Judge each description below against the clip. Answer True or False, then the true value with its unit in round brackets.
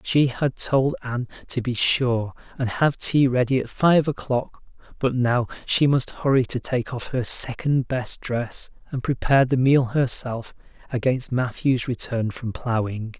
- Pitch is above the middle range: False (125 Hz)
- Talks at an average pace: True (165 wpm)